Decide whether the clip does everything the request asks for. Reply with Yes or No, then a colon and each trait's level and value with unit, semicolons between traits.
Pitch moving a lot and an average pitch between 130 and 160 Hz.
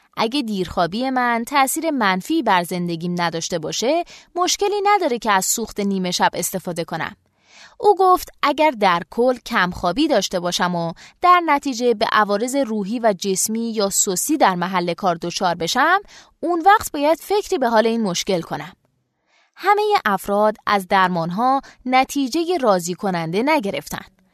No: wide, 8.0 semitones; high, 215 Hz